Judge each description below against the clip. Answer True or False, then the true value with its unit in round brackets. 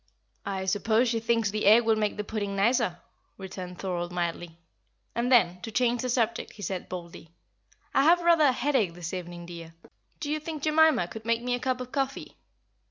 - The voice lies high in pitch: True (220 Hz)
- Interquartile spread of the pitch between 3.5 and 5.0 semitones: False (5.6 semitones)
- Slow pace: False (195 wpm)